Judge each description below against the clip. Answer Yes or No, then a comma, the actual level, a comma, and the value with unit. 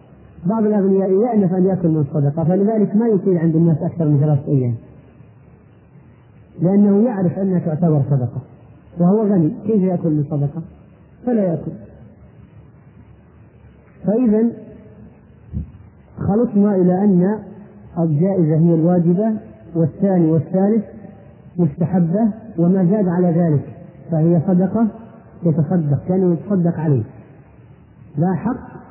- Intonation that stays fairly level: No, average, 4.6 semitones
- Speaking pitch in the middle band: Yes, medium, 170 Hz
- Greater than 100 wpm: Yes, average, 110 wpm